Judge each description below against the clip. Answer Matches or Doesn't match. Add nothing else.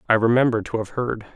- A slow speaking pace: Doesn't match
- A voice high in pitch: Doesn't match